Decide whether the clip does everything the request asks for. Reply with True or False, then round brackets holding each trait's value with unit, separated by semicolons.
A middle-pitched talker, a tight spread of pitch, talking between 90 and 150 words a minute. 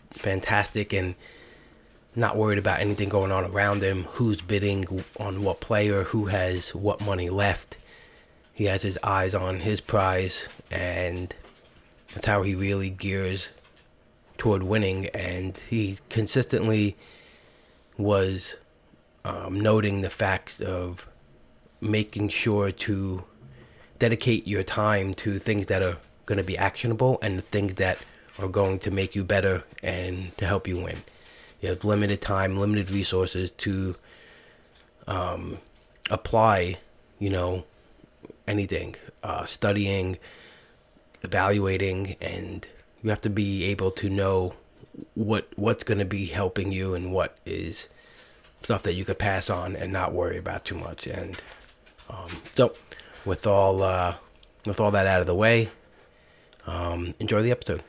False (100 Hz; 1.9 semitones; 140 wpm)